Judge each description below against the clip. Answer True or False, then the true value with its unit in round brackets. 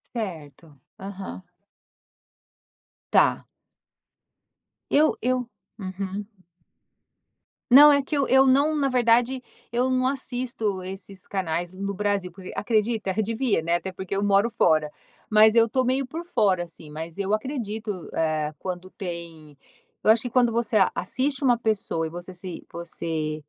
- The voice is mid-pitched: False (205 Hz)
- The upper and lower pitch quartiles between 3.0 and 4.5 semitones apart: False (5.6 semitones)